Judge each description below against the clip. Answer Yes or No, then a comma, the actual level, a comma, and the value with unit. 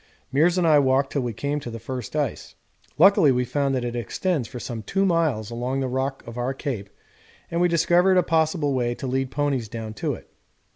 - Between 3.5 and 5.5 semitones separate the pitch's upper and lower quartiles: Yes, average, 4.6 semitones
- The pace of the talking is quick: Yes, fast, 220 wpm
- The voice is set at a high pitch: No, low, 135 Hz